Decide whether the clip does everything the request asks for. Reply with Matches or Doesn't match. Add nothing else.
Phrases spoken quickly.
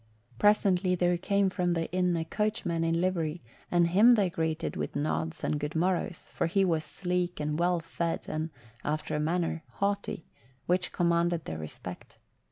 Doesn't match